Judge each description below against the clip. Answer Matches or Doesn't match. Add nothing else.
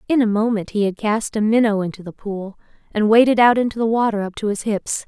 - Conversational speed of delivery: Doesn't match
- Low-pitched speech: Doesn't match